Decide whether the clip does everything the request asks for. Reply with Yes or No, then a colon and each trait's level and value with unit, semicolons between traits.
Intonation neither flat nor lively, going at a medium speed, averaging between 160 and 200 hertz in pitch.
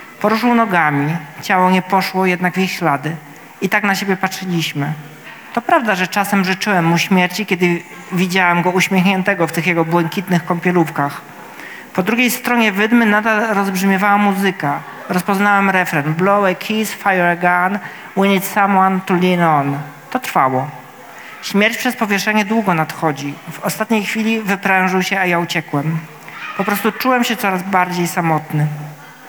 Yes: average, 3.1 semitones; average, 150 wpm; medium, 185 Hz